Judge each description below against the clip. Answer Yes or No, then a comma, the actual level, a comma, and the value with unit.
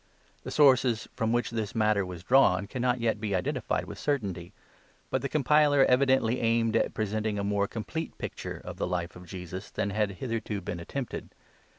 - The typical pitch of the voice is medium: No, low, 110 Hz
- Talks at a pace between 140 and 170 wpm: No, average, 185 wpm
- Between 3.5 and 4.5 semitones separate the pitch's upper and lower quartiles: Yes, average, 4.2 semitones